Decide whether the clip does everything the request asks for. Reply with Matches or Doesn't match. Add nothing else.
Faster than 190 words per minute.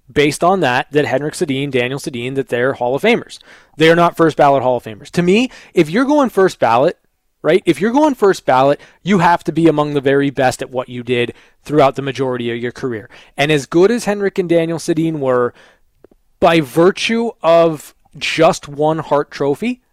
Matches